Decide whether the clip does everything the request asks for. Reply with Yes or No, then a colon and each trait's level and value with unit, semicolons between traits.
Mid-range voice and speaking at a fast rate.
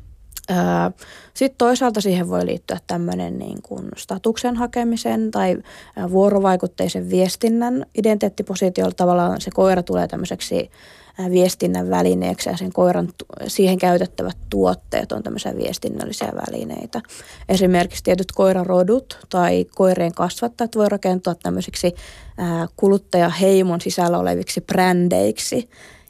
No: medium, 180 Hz; average, 100 wpm